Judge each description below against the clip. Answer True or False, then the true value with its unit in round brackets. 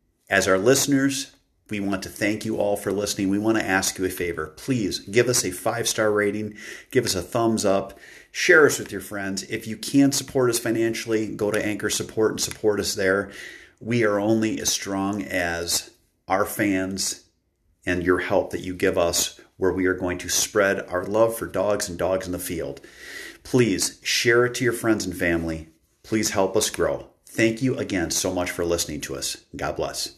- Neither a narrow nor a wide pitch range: True (3.6 semitones)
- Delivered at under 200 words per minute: False (205 wpm)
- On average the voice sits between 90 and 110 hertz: True (100 Hz)